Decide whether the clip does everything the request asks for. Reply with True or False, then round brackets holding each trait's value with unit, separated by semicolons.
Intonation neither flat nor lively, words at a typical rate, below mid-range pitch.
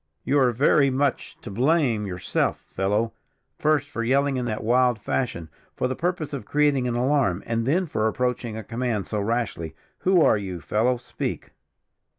True (4.4 semitones; 170 wpm; 125 Hz)